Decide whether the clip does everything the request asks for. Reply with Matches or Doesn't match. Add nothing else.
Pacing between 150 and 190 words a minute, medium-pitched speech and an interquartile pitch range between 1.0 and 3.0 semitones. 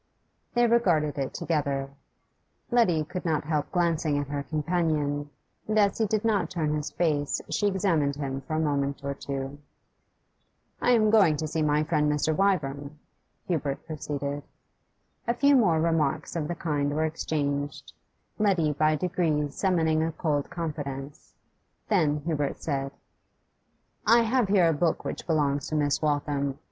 Doesn't match